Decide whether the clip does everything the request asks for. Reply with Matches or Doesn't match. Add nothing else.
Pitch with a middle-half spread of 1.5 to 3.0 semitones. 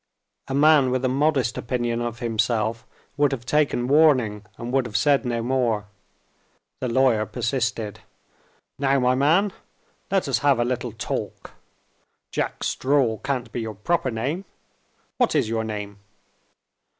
Doesn't match